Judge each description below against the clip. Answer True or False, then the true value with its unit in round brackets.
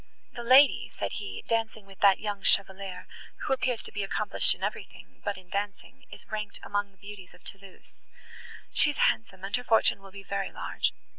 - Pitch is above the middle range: True (200 Hz)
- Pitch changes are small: True (2.3 semitones)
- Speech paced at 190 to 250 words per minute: True (195 wpm)